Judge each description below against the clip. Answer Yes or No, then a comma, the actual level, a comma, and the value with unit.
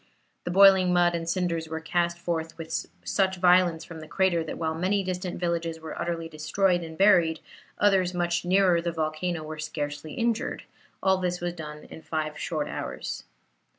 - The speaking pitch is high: No, medium, 170 Hz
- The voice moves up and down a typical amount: No, narrow, 2.2 semitones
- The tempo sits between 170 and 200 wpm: Yes, average, 180 wpm